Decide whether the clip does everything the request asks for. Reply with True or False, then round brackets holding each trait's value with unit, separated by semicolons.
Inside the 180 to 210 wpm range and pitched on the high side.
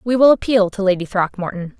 True (200 wpm; 205 Hz)